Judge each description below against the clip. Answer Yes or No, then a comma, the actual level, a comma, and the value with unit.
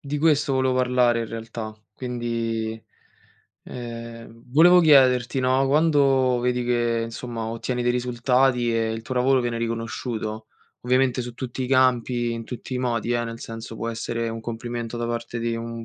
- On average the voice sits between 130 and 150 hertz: No, low, 120 Hz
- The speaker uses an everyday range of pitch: No, narrow, 1.8 semitones